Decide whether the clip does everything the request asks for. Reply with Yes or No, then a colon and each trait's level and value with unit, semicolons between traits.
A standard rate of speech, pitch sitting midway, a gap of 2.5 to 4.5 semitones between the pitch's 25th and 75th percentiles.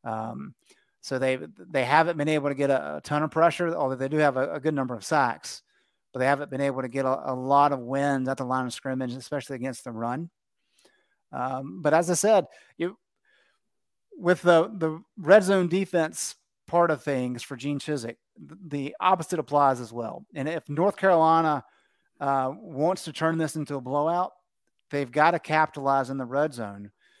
Yes: average, 195 wpm; medium, 145 Hz; average, 3.7 semitones